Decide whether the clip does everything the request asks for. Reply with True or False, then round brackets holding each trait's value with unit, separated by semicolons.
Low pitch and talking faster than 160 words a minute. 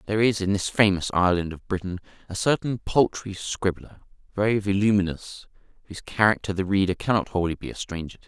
True (100 Hz; 175 wpm)